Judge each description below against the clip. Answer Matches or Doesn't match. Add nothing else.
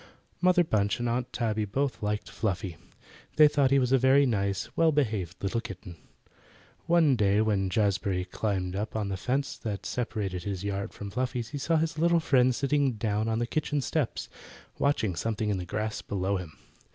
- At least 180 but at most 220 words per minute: Matches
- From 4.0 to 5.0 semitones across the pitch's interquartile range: Doesn't match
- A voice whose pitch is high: Doesn't match